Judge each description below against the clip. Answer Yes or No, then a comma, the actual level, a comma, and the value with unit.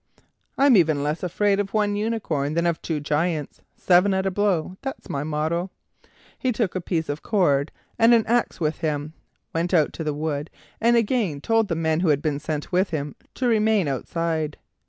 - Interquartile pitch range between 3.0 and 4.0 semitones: No, average, 5.2 semitones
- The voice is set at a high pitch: No, medium, 170 Hz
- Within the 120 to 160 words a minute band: No, average, 195 wpm